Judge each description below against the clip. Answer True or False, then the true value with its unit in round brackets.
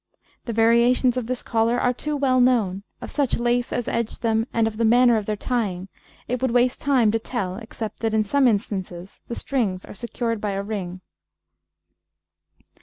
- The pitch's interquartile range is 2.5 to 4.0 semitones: True (2.8 semitones)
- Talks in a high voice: True (230 Hz)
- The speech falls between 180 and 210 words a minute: True (185 wpm)